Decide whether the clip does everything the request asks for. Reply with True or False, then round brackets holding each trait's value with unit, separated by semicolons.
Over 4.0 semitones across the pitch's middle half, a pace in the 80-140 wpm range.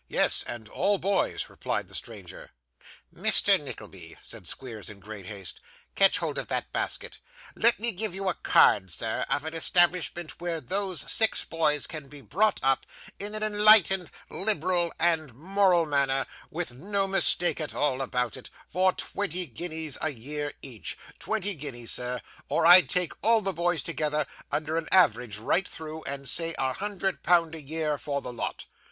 False (5.6 semitones; 170 wpm)